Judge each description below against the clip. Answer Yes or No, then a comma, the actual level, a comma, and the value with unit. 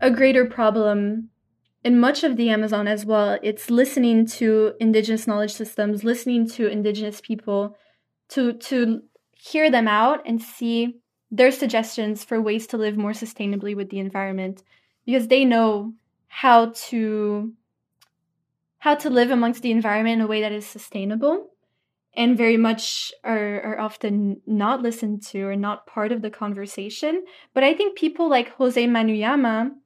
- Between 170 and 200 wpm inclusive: No, average, 155 wpm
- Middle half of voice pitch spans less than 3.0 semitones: Yes, narrow, 2.6 semitones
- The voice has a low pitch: No, high, 225 Hz